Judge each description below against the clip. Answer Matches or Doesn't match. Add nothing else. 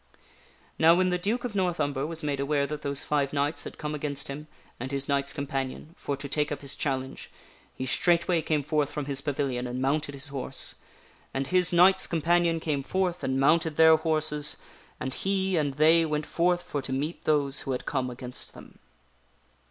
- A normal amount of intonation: Matches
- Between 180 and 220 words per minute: Matches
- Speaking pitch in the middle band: Matches